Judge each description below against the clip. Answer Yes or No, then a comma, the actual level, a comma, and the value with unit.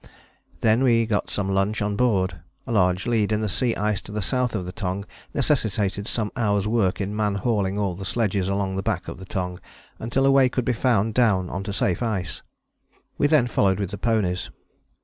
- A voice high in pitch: No, low, 105 Hz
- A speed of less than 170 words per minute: No, fast, 205 wpm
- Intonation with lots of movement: No, average, 3.1 semitones